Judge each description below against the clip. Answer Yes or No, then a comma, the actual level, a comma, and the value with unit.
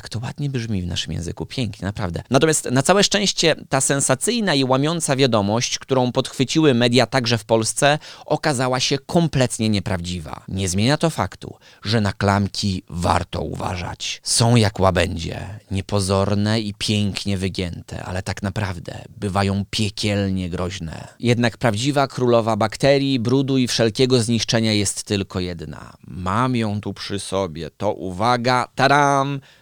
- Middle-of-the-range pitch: No, low, 110 Hz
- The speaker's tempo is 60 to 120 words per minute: No, average, 140 wpm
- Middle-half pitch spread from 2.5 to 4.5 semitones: No, average, 5.3 semitones